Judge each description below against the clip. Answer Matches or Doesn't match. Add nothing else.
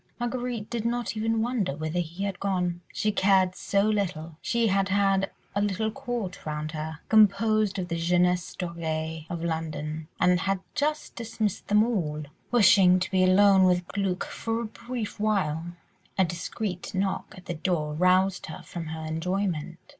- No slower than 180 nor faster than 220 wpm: Doesn't match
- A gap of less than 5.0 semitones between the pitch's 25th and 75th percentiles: Matches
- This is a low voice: Doesn't match